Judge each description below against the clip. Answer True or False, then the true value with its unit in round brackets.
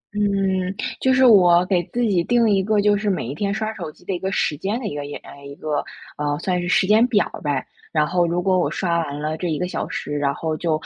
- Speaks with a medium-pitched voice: True (180 Hz)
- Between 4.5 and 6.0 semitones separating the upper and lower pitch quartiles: True (4.8 semitones)